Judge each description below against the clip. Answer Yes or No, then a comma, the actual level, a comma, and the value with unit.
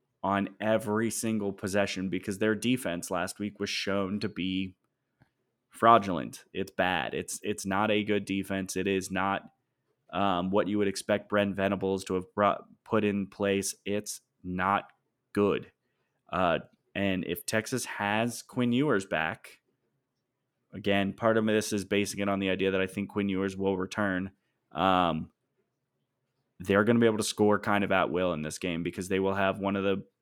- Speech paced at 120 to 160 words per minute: No, average, 175 wpm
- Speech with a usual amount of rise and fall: No, narrow, 1.5 semitones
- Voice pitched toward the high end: No, low, 100 Hz